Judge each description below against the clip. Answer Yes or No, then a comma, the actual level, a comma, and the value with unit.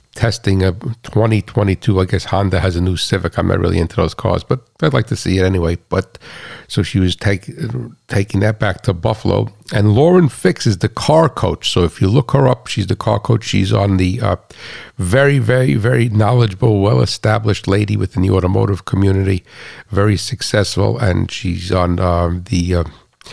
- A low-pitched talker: Yes, low, 100 Hz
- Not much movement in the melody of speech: No, average, 3.6 semitones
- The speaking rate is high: No, average, 190 wpm